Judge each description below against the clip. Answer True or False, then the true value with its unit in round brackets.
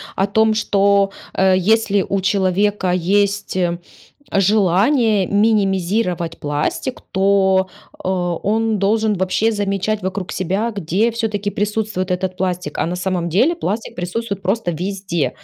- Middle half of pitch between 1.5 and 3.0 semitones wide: True (2.6 semitones)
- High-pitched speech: True (195 Hz)